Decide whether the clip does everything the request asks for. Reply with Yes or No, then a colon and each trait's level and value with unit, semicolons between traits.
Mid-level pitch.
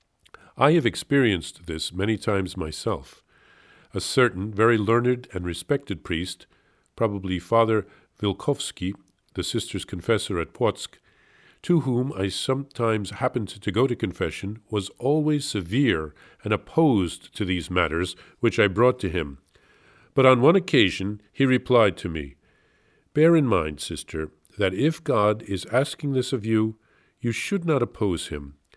No: low, 105 Hz